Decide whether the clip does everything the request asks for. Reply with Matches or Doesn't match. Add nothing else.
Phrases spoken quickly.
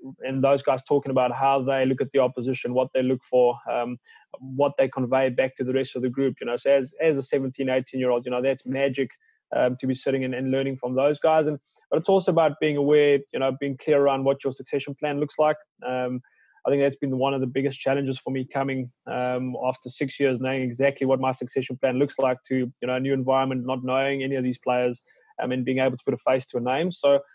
Matches